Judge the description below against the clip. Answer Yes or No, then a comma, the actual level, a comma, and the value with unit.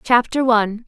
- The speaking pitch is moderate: No, high, 230 Hz